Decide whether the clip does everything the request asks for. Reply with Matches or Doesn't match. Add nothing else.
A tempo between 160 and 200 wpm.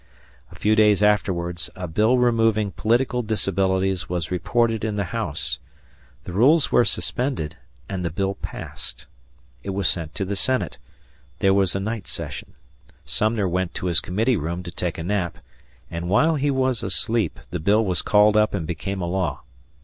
Matches